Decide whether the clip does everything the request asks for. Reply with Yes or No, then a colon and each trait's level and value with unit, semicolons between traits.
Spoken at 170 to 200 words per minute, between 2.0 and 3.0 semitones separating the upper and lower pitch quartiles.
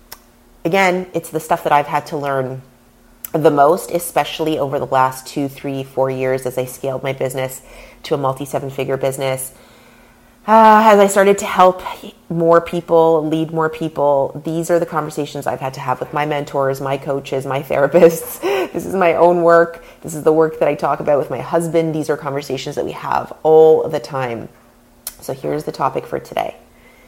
No: average, 195 wpm; average, 3.8 semitones